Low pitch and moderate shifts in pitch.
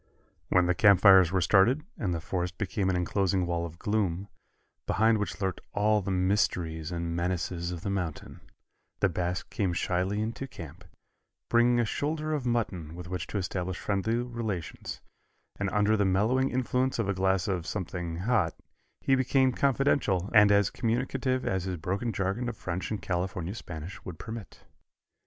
Yes: very low, 95 Hz; average, 4.1 semitones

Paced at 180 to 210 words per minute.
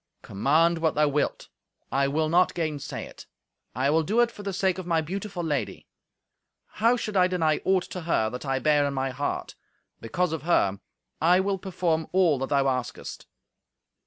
Yes: average, 185 wpm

